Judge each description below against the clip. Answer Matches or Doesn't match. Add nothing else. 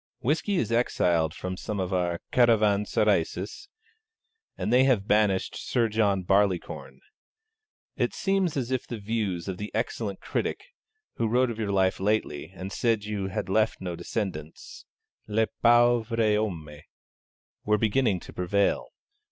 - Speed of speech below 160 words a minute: Matches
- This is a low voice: Matches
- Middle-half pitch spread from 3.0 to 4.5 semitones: Matches